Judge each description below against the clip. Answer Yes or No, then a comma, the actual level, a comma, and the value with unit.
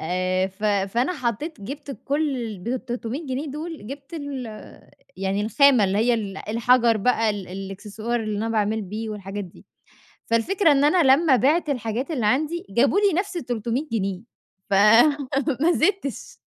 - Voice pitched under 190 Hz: No, high, 240 Hz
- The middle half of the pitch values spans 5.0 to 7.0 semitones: Yes, wide, 5.5 semitones